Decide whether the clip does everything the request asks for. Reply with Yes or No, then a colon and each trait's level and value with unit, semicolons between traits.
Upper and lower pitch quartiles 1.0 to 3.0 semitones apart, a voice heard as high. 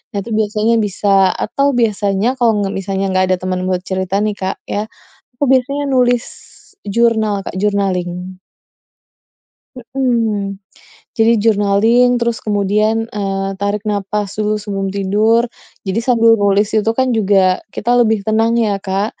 Yes: narrow, 2.6 semitones; high, 210 Hz